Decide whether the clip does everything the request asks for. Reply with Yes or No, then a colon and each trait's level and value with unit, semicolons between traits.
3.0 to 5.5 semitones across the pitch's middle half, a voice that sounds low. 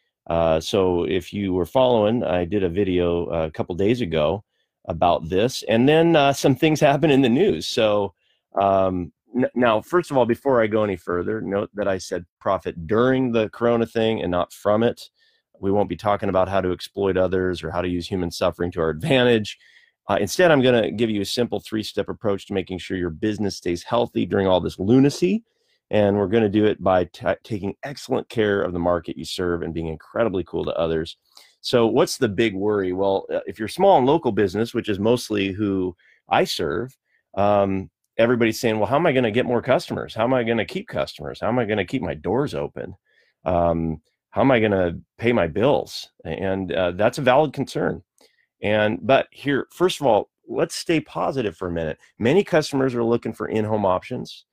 Yes: average, 4.7 semitones; low, 105 Hz